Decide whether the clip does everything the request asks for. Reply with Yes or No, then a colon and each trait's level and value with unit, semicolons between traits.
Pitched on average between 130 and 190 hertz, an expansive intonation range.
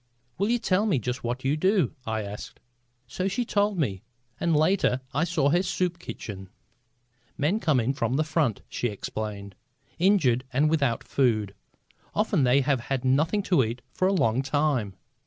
Yes: medium, 140 Hz; wide, 6.7 semitones